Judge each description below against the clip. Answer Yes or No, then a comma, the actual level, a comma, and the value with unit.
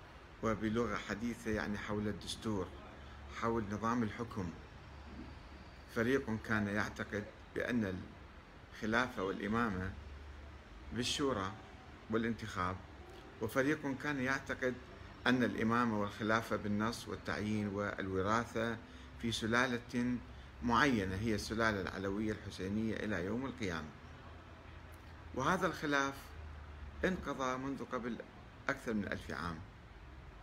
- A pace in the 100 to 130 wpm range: No, average, 85 wpm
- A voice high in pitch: No, low, 105 Hz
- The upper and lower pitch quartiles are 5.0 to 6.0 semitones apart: Yes, wide, 5.5 semitones